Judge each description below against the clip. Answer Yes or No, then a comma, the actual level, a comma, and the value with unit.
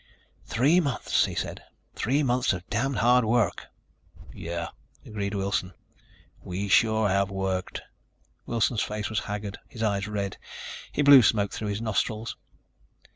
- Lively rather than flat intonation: No, average, 3.1 semitones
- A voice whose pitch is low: Yes, low, 105 Hz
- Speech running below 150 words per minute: Yes, slow, 135 wpm